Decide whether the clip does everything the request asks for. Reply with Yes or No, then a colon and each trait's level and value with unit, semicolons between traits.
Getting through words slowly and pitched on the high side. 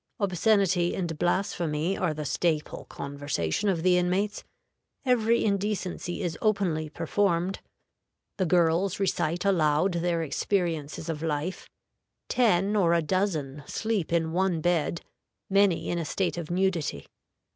No: slow, 125 wpm; medium, 175 Hz